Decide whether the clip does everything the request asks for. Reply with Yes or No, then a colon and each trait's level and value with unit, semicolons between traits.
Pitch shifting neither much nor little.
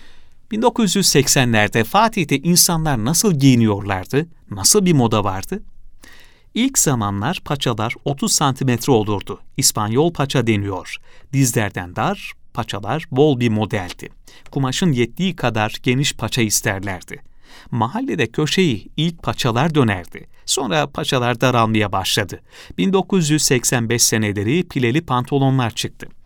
No: wide, 6.2 semitones